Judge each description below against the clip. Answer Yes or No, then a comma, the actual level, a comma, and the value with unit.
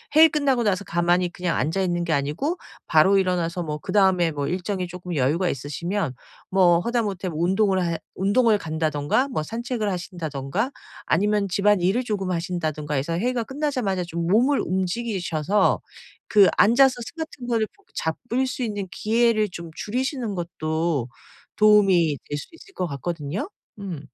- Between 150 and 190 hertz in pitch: Yes, medium, 185 Hz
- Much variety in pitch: No, average, 4.8 semitones